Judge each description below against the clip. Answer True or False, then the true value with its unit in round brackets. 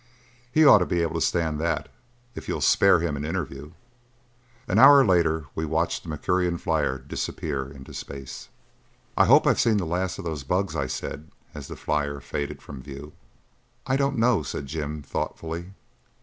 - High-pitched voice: False (80 Hz)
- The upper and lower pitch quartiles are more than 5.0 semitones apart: False (3.9 semitones)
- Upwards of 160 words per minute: True (175 wpm)